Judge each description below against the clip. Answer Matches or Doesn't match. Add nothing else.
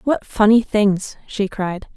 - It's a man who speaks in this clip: Doesn't match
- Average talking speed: Matches